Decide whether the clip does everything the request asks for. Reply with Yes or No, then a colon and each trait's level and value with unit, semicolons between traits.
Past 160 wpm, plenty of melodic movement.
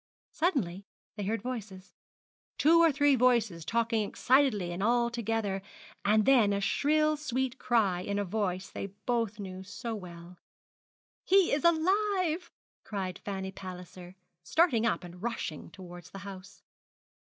No: average, 140 wpm; wide, 5.7 semitones